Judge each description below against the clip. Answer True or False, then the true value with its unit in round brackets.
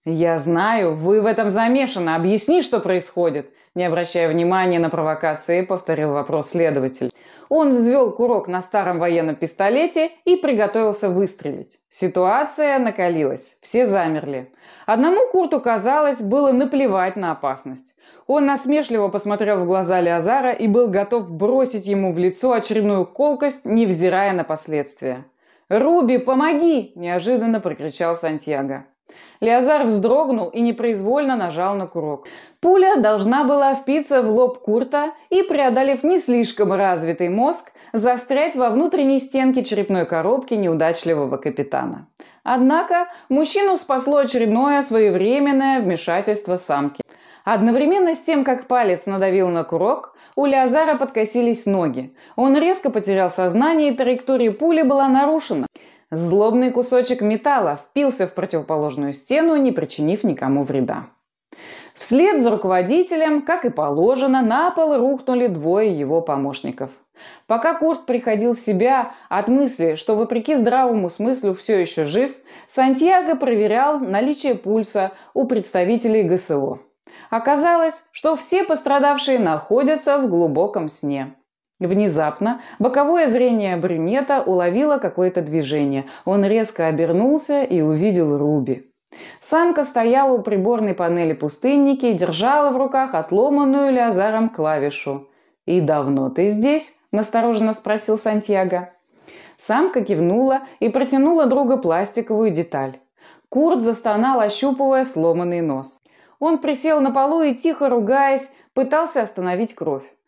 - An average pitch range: False (7.5 semitones)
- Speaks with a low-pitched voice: False (225 Hz)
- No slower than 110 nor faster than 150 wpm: True (120 wpm)